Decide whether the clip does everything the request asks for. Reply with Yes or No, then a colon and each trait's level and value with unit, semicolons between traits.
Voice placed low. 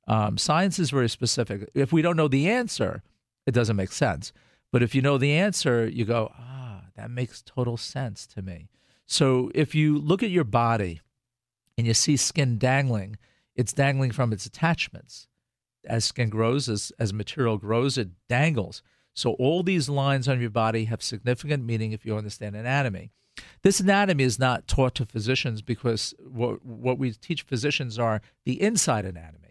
Yes: low, 125 Hz